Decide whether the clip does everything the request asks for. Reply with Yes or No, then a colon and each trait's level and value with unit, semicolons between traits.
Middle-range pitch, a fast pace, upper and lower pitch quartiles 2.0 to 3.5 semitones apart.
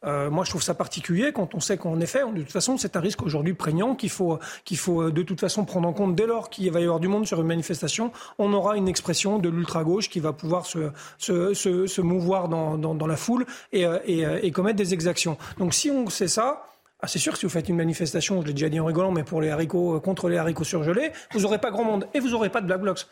Yes: medium, 180 Hz; fast, 275 wpm; average, 3.1 semitones